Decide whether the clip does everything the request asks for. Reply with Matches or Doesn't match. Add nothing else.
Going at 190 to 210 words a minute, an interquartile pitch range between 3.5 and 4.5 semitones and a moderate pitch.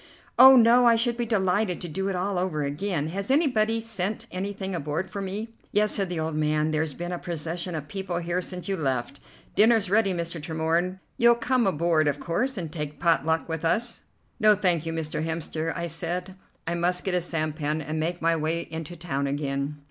Matches